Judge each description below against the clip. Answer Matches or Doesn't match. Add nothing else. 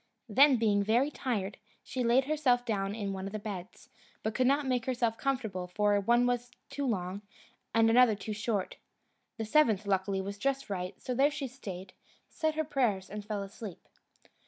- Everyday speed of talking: Matches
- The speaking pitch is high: Matches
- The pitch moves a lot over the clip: Doesn't match